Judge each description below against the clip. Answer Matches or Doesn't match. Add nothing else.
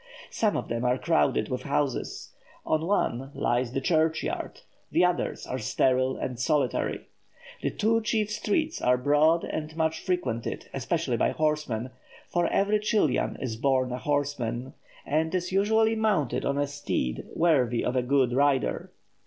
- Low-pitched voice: Doesn't match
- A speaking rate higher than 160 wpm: Doesn't match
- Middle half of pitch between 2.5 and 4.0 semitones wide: Doesn't match